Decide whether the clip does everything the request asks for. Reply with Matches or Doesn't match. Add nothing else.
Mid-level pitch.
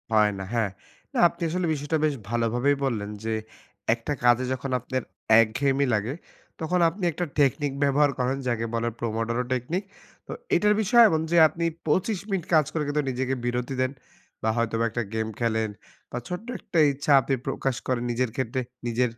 Doesn't match